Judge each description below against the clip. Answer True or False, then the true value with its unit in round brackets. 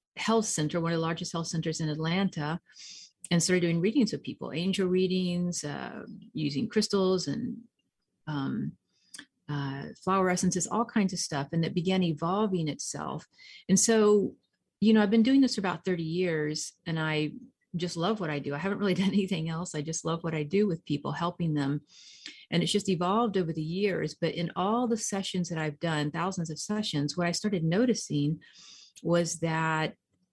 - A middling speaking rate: True (185 wpm)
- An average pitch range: True (4.3 semitones)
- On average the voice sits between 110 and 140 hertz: False (180 Hz)